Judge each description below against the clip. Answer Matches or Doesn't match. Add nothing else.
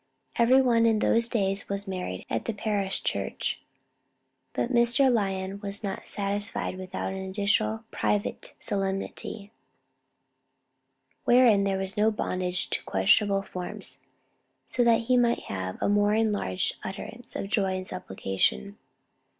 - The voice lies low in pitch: Doesn't match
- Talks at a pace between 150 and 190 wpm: Doesn't match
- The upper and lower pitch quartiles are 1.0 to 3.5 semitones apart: Matches